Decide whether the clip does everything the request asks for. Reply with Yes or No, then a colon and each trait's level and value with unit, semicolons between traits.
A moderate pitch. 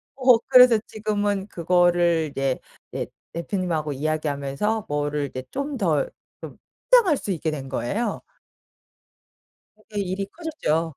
Yes: medium, 175 Hz